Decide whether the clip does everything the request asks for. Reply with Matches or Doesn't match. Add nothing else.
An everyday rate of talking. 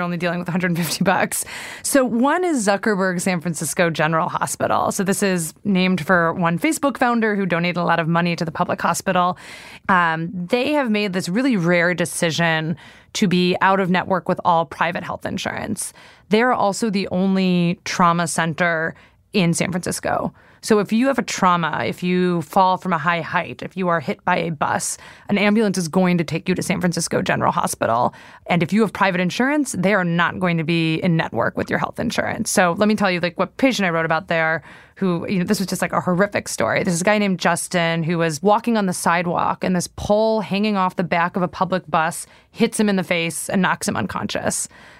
Doesn't match